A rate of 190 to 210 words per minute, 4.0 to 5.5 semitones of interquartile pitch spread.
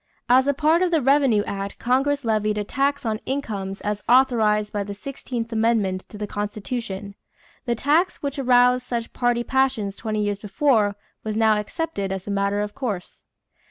No: average, 175 wpm; average, 4.3 semitones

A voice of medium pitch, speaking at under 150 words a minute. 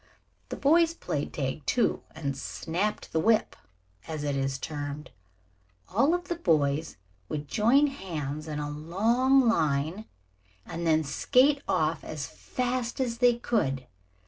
Yes: medium, 170 Hz; average, 140 wpm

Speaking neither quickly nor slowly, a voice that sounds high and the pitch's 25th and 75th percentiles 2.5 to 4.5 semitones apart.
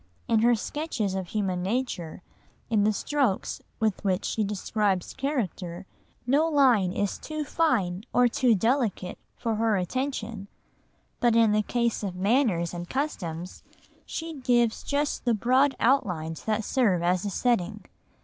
No: average, 145 wpm; high, 220 Hz; average, 5.2 semitones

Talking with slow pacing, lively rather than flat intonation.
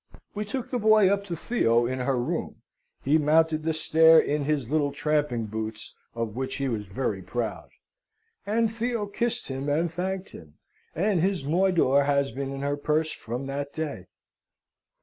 No: average, 170 wpm; wide, 5.7 semitones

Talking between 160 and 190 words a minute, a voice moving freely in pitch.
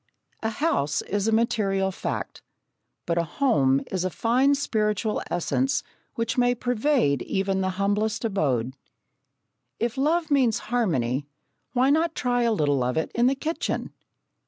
No: average, 145 wpm; wide, 6.0 semitones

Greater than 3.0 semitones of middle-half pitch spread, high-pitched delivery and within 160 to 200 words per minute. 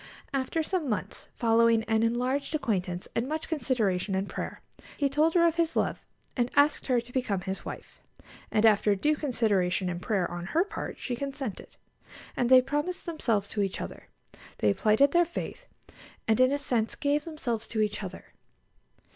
Yes: wide, 5.6 semitones; high, 245 Hz; average, 175 wpm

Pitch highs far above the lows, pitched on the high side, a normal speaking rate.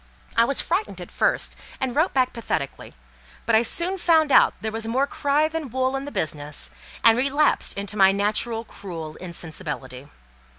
Yes: wide, 6.5 semitones; high, 230 Hz; average, 170 wpm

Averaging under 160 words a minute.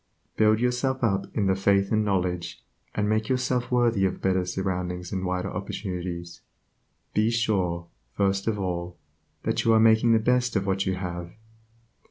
No: average, 165 wpm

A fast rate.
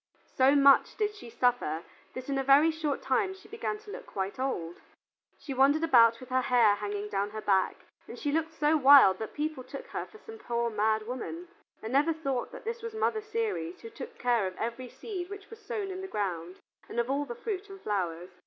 Yes: fast, 220 wpm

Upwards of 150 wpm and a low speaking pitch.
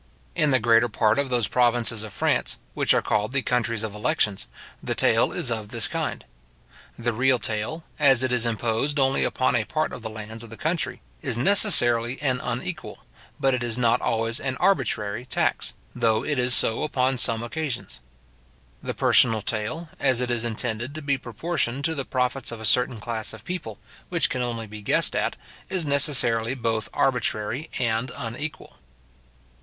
Yes: average, 180 wpm; low, 120 Hz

